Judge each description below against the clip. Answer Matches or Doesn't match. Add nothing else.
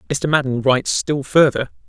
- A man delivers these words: Matches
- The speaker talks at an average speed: Matches